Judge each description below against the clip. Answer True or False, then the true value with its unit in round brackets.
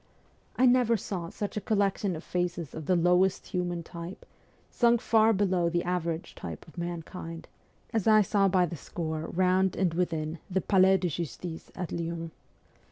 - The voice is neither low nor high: True (180 Hz)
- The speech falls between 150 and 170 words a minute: True (165 wpm)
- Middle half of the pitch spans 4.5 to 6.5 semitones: False (2.4 semitones)